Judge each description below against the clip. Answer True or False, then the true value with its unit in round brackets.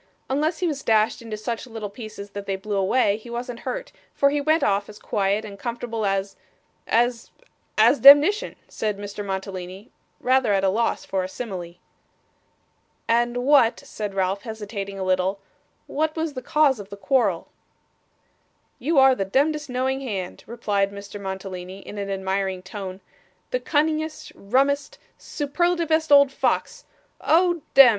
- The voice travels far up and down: True (5.9 semitones)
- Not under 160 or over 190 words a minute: False (150 wpm)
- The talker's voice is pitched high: True (225 Hz)